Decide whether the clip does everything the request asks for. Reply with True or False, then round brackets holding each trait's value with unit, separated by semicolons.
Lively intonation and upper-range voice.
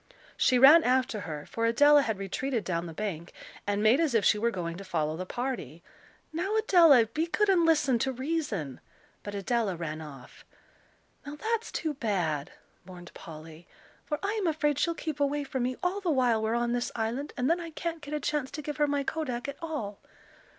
True (7.3 semitones; 250 Hz)